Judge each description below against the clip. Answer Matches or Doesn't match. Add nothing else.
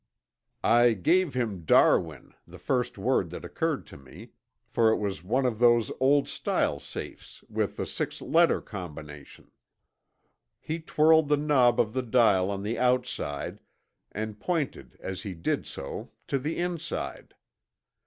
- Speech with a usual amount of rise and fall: Doesn't match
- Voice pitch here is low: Matches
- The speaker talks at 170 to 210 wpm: Doesn't match